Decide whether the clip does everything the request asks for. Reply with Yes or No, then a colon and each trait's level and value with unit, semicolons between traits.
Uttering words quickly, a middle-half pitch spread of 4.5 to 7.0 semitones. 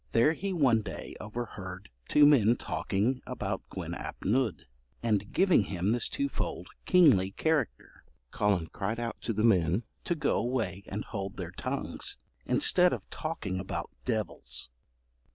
No: average, 145 wpm; wide, 5.4 semitones